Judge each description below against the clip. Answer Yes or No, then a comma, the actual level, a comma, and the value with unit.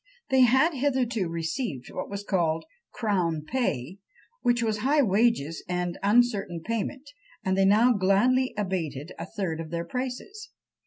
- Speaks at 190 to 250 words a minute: No, average, 145 wpm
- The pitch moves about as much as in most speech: No, wide, 6.4 semitones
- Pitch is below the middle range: No, high, 205 Hz